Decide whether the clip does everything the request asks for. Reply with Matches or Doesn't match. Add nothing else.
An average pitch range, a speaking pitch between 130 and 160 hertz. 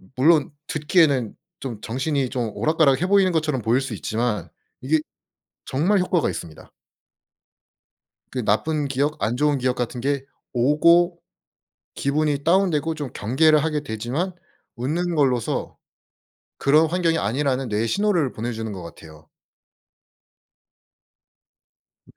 Matches